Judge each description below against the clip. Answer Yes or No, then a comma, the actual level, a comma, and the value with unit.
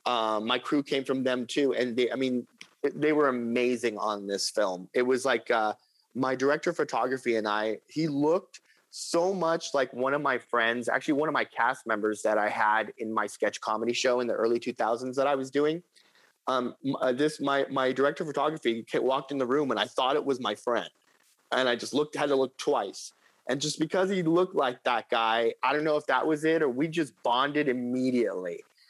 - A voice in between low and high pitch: No, low, 130 Hz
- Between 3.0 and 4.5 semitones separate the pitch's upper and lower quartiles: Yes, average, 3.9 semitones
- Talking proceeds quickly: Yes, fast, 215 wpm